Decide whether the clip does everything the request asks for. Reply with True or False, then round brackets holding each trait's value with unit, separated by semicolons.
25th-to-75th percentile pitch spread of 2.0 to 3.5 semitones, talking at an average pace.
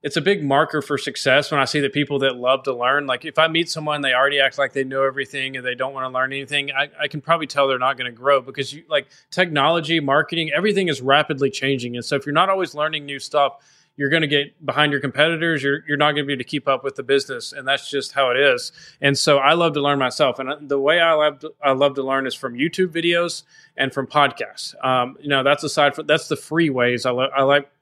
False (2.5 semitones; 270 wpm)